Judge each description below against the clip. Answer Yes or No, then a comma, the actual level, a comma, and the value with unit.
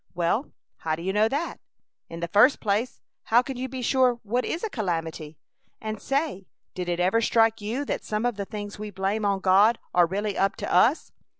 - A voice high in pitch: Yes, high, 210 Hz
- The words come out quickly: Yes, fast, 210 wpm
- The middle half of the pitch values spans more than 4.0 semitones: Yes, average, 4.4 semitones